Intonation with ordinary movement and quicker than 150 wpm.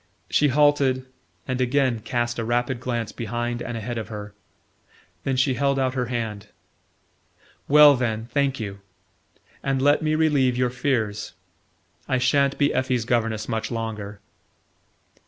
No: average, 3.1 semitones; average, 140 wpm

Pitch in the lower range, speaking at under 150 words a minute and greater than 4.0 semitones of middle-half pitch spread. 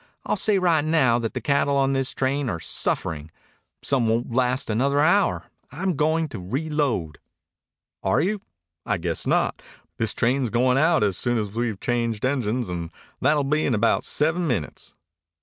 No: low, 130 Hz; average, 165 wpm; average, 4.9 semitones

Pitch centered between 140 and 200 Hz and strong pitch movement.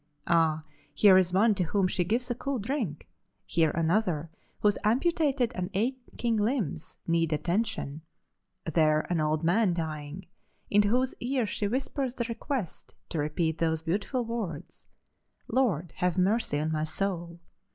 Yes: medium, 185 Hz; wide, 6.2 semitones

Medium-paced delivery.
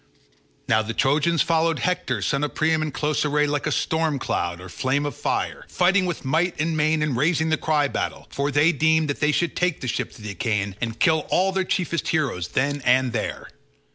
No: fast, 215 wpm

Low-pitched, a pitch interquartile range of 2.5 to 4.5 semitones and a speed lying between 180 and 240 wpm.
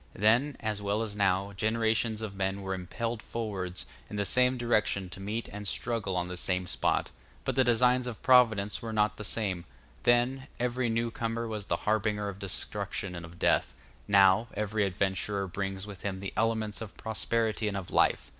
Yes: low, 105 Hz; average, 2.8 semitones; average, 185 wpm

